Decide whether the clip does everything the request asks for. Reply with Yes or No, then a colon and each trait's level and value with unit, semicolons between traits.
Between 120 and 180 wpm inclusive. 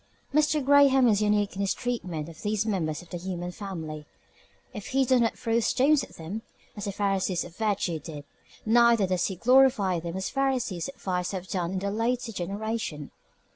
No: average, 195 wpm